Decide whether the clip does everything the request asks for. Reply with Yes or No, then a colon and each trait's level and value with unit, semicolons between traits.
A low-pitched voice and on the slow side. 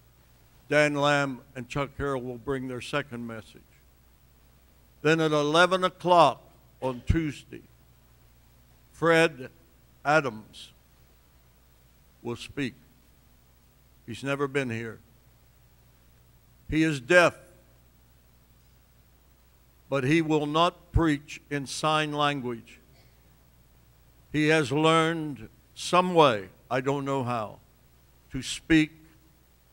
Yes: low, 120 Hz; slow, 95 wpm